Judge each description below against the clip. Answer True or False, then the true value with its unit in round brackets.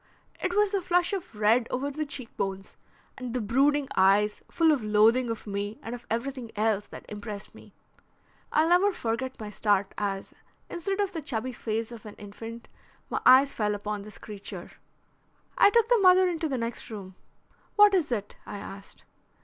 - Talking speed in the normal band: True (180 wpm)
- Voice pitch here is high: True (235 Hz)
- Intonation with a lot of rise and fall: True (6.8 semitones)